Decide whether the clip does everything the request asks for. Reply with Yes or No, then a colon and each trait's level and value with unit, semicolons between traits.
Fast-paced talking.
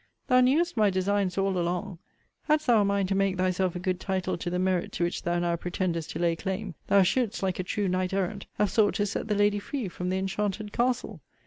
Yes: fast, 235 wpm